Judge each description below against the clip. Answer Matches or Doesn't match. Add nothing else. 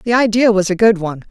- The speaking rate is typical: Doesn't match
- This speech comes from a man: Doesn't match